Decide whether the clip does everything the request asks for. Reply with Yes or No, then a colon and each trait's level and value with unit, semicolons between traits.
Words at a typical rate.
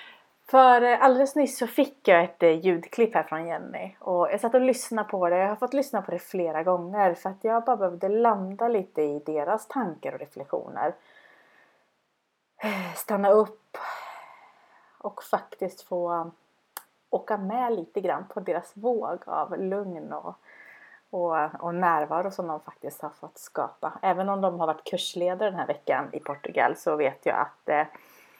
Yes: average, 160 wpm